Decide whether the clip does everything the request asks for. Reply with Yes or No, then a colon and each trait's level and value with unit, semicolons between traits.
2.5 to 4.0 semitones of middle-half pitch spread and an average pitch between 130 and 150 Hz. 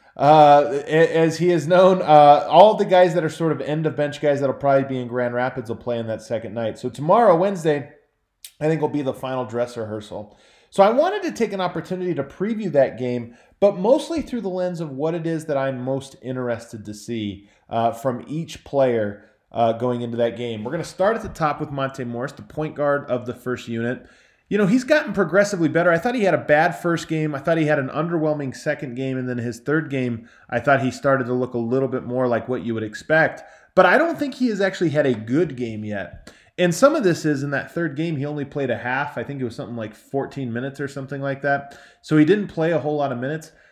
No: average, 5.1 semitones; medium, 140 Hz